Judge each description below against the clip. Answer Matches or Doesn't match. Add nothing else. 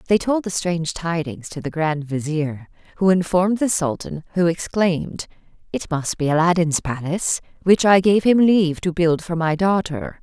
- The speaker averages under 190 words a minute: Matches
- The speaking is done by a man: Doesn't match